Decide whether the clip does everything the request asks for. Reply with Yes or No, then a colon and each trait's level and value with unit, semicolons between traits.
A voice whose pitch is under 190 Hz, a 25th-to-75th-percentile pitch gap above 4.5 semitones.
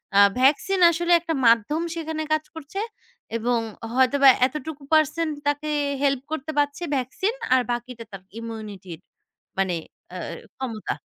No: very high, 275 Hz; average, 5.1 semitones